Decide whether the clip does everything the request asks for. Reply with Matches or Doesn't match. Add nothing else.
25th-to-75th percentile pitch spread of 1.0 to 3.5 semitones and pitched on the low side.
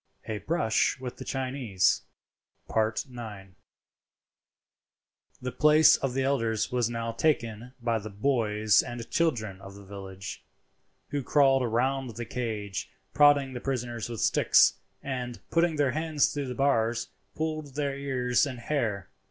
Doesn't match